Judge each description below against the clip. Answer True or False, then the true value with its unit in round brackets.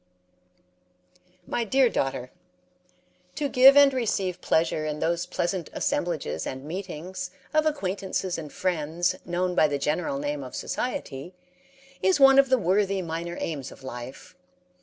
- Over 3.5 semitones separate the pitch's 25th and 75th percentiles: True (4.9 semitones)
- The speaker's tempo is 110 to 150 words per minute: True (140 wpm)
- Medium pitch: True (175 Hz)